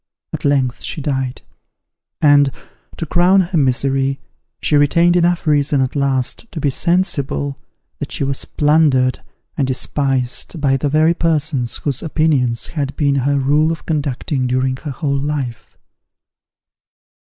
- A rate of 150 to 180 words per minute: No, average, 140 wpm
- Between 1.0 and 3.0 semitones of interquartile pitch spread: Yes, average, 2.7 semitones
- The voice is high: No, medium, 140 Hz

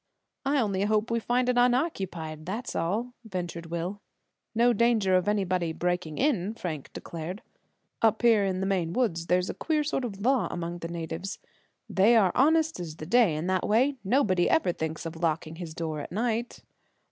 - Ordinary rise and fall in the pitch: No, wide, 5.7 semitones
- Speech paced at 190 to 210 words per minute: No, average, 180 wpm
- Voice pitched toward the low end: No, high, 190 Hz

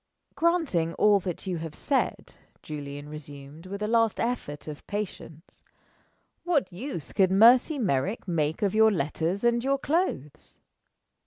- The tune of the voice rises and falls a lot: Yes, wide, 7.5 semitones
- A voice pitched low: No, high, 190 Hz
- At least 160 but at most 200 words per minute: No, average, 140 wpm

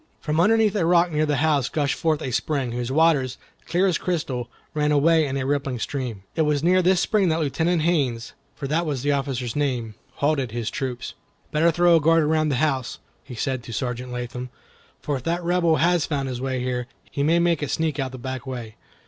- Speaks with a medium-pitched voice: Yes, medium, 145 Hz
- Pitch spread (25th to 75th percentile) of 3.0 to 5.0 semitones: Yes, average, 4.2 semitones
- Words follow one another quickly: Yes, fast, 215 wpm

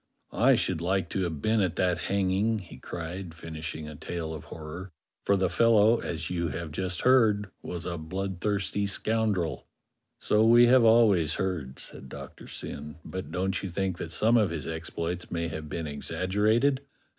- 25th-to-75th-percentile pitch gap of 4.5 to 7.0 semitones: No, average, 3.9 semitones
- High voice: No, very low, 90 Hz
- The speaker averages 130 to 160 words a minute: No, average, 170 wpm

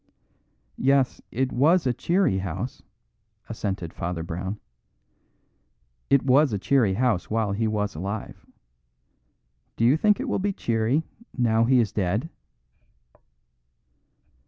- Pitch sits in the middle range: No, low, 115 Hz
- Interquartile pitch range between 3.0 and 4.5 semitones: No, wide, 5.5 semitones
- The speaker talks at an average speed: No, slow, 120 wpm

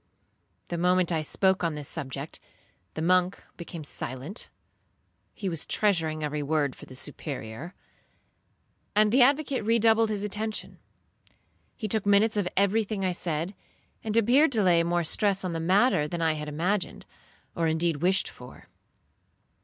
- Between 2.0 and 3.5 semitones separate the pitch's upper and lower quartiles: No, average, 4.8 semitones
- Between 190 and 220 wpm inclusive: No, average, 155 wpm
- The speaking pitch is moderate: Yes, medium, 180 Hz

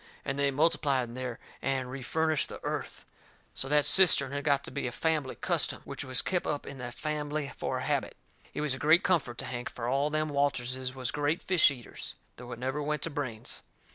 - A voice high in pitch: No, medium, 140 Hz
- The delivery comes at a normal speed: No, fast, 215 wpm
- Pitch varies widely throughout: No, average, 2.8 semitones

